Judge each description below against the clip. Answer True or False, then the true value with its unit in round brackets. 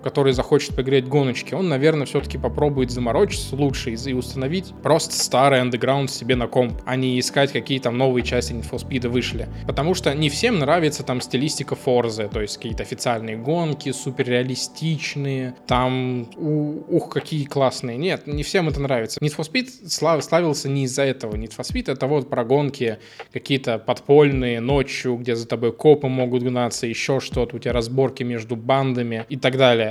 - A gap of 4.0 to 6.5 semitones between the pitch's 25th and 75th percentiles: False (2.8 semitones)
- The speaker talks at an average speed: False (175 wpm)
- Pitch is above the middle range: False (130 Hz)